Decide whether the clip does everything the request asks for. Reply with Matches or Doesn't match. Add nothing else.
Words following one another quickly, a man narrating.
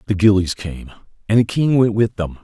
Matches